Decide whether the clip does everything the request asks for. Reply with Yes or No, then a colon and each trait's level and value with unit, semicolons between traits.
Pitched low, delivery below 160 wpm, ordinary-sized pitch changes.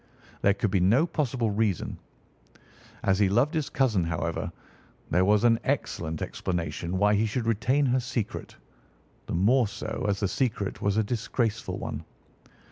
Yes: low, 105 Hz; average, 150 wpm; average, 4.3 semitones